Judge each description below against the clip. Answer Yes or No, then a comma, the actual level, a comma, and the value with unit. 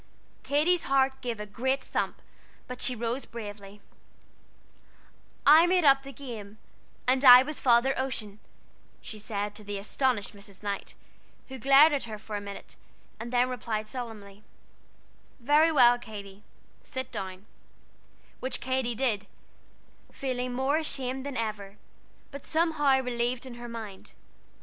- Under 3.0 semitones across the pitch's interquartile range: No, average, 4.1 semitones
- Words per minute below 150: Yes, average, 140 wpm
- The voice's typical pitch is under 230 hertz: No, high, 245 Hz